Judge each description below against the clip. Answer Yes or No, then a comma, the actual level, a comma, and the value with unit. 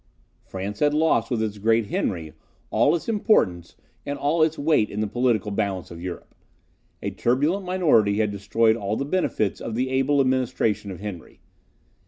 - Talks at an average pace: Yes, average, 170 wpm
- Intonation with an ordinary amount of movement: No, wide, 5.9 semitones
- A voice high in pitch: No, low, 115 Hz